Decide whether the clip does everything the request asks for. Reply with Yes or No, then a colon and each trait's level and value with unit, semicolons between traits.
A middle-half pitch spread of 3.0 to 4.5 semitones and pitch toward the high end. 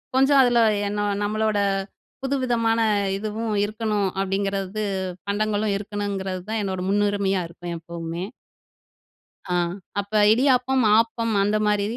No: narrow, 2.5 semitones; high, 210 Hz